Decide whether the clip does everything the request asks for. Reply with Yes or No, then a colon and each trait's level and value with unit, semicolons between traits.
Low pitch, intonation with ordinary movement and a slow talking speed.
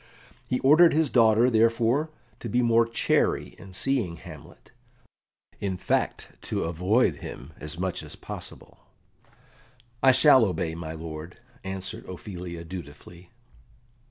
No: very low, 95 Hz; wide, 5.9 semitones; slow, 125 wpm